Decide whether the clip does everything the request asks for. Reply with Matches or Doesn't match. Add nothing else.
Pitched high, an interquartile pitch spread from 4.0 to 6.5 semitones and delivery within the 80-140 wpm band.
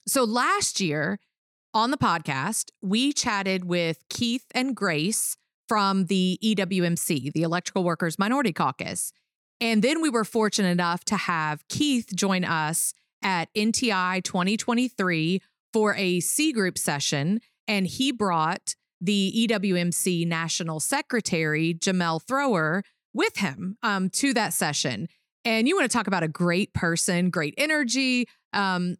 Matches